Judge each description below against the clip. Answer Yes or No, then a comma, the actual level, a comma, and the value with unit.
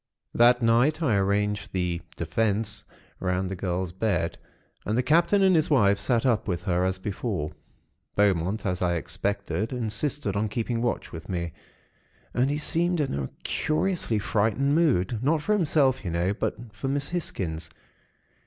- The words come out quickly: No, average, 160 wpm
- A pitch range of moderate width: No, wide, 6.4 semitones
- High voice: No, low, 105 Hz